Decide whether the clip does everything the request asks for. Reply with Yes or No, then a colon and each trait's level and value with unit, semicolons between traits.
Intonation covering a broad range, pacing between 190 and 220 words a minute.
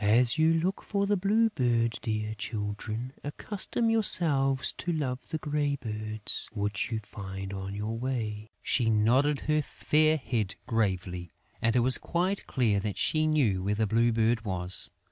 No: wide, 6.1 semitones; average, 165 wpm